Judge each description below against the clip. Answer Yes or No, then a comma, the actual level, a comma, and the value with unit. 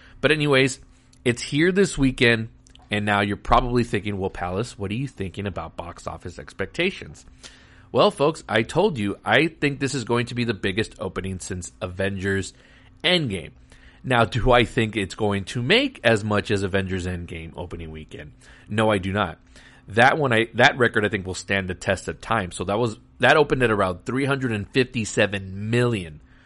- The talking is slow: No, average, 180 wpm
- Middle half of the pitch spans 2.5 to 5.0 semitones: Yes, average, 4.2 semitones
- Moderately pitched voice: No, low, 105 Hz